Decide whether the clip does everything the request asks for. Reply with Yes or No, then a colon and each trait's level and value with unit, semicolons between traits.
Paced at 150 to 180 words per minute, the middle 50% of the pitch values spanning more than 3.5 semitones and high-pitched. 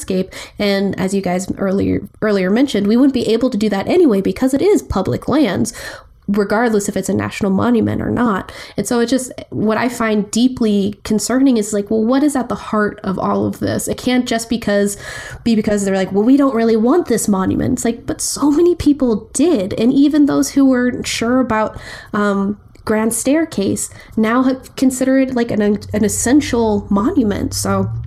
No: average, 200 wpm; average, 4.2 semitones; high, 225 Hz